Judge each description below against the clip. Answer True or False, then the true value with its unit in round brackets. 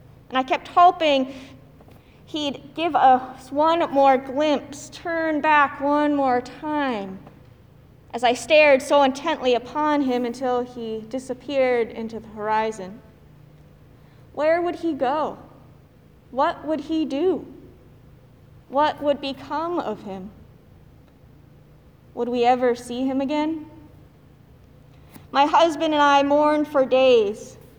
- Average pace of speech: False (115 wpm)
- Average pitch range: True (3.8 semitones)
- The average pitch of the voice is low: False (275 Hz)